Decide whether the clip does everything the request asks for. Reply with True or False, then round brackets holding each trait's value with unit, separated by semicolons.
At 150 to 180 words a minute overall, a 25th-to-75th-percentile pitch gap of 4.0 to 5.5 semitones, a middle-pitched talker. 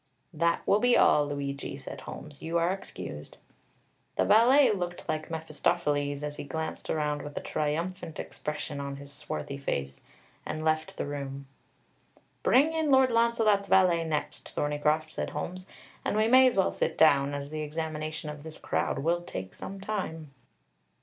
True (165 wpm; 4.3 semitones; 155 Hz)